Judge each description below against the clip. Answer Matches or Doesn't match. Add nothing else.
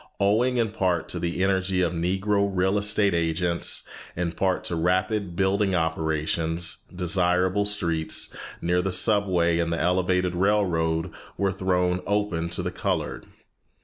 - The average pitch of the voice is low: Matches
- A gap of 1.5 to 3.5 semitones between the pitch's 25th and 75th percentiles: Matches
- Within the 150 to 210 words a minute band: Doesn't match